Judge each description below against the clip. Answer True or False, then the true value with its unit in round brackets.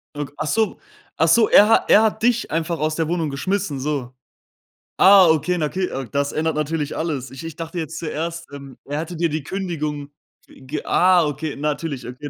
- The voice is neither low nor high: True (160 Hz)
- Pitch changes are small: False (3.2 semitones)